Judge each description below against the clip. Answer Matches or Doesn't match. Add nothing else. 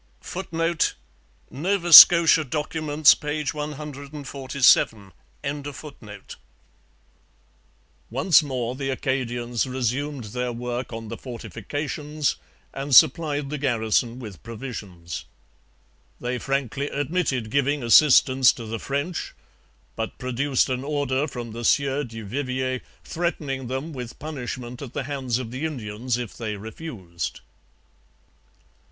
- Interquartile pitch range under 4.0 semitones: Matches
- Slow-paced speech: Matches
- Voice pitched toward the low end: Matches